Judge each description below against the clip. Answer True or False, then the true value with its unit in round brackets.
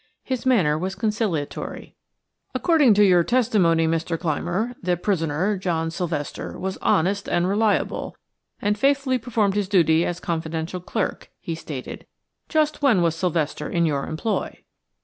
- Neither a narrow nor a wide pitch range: True (4.6 semitones)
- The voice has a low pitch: False (180 Hz)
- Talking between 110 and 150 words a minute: True (140 wpm)